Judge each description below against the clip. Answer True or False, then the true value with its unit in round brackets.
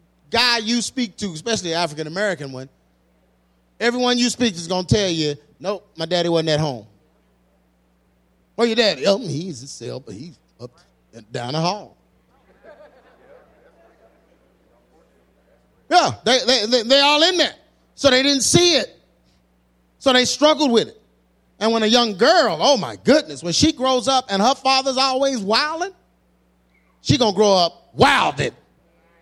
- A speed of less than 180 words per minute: True (160 wpm)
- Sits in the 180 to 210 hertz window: True (190 Hz)